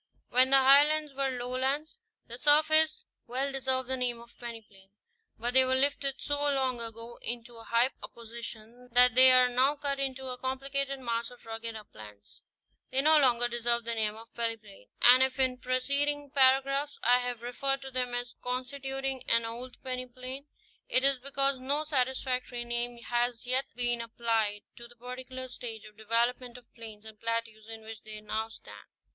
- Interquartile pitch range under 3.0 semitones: Yes, narrow, 2.5 semitones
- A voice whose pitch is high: Yes, very high, 250 Hz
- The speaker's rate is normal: Yes, average, 180 wpm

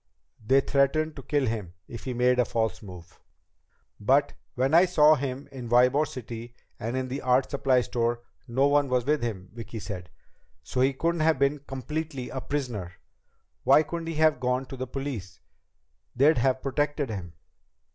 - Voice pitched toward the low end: Yes, low, 130 Hz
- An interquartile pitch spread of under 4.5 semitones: Yes, average, 3.3 semitones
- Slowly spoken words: No, average, 175 wpm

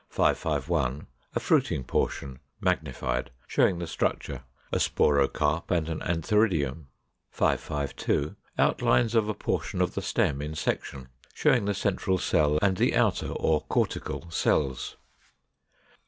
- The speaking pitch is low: Yes, very low, 80 Hz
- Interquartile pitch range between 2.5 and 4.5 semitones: No, average, 4.9 semitones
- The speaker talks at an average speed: No, slow, 125 wpm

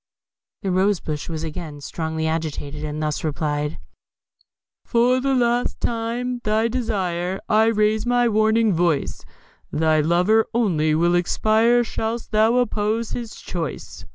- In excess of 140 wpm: No, slow, 135 wpm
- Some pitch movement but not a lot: No, wide, 6.3 semitones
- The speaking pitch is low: No, high, 210 Hz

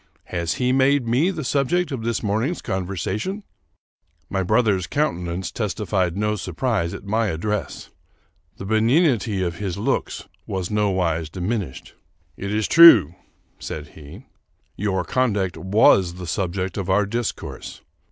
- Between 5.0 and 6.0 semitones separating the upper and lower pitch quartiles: No, average, 4.4 semitones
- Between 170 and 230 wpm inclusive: No, average, 140 wpm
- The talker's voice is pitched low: Yes, low, 100 Hz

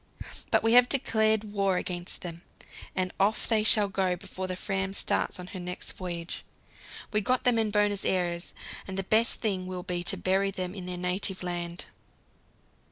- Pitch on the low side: No, high, 190 Hz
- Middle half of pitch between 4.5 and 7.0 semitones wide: No, narrow, 2.6 semitones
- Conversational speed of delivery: Yes, average, 180 wpm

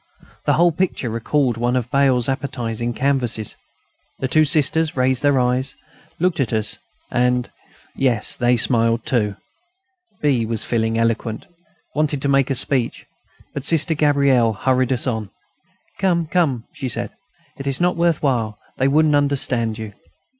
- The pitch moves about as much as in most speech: Yes, average, 3.5 semitones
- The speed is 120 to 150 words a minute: Yes, average, 145 wpm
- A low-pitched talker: Yes, low, 130 Hz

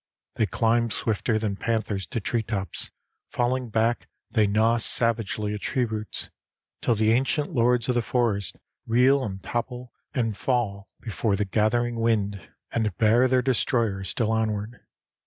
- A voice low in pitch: Yes, low, 115 Hz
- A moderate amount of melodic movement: No, narrow, 2.3 semitones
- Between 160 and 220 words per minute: No, average, 145 wpm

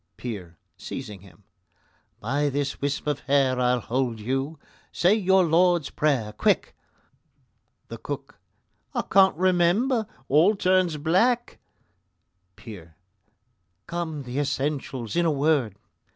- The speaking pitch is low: No, medium, 145 Hz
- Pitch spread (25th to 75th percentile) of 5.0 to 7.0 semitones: Yes, wide, 5.6 semitones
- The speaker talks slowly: Yes, slow, 115 wpm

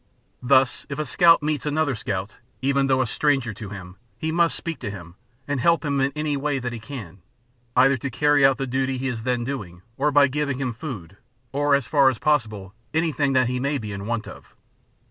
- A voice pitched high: No, low, 135 Hz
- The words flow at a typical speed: No, fast, 220 wpm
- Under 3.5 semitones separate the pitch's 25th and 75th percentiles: No, average, 4.1 semitones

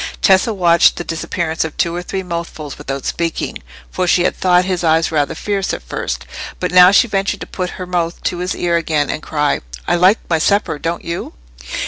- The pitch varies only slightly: Yes, narrow, 2.0 semitones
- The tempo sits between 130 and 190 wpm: No, fast, 205 wpm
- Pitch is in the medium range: Yes, medium, 175 Hz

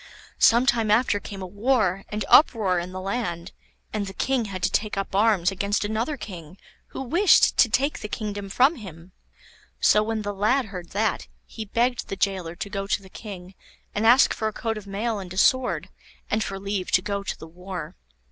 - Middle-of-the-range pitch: No, high, 205 Hz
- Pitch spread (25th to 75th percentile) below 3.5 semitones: Yes, average, 2.9 semitones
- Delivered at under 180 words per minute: No, fast, 205 wpm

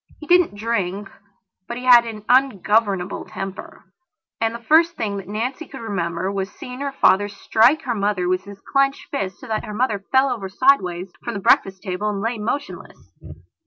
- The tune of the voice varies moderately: Yes, average, 4.5 semitones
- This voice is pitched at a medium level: No, high, 215 Hz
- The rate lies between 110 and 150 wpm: No, average, 185 wpm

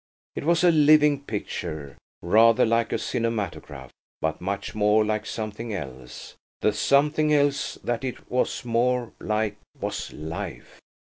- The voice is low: Yes, low, 115 Hz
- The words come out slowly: Yes, slow, 130 wpm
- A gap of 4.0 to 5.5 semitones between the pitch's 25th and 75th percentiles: Yes, average, 5.1 semitones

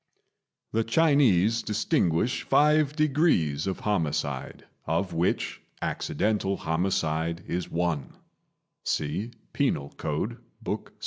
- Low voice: Yes, very low, 95 Hz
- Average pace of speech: No, slow, 100 wpm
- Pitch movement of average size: No, wide, 6.4 semitones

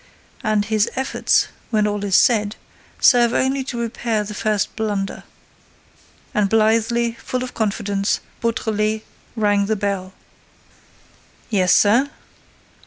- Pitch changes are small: Yes, narrow, 2.2 semitones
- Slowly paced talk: Yes, slow, 115 wpm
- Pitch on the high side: Yes, high, 215 Hz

